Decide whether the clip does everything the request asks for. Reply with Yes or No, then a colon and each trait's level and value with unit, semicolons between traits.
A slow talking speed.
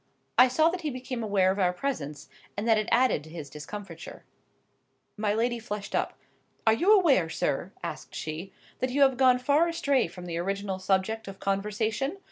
No: average, 185 wpm